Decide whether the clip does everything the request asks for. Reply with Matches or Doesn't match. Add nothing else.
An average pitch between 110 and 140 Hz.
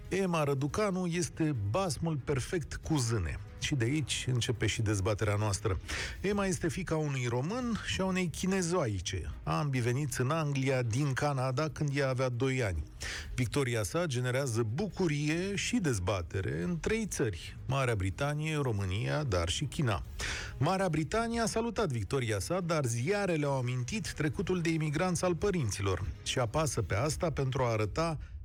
Matches